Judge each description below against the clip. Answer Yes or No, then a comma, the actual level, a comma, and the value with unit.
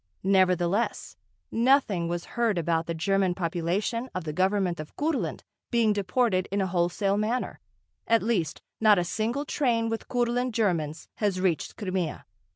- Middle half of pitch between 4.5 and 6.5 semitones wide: Yes, average, 4.8 semitones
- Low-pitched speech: No, high, 195 Hz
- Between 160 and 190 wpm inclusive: No, average, 150 wpm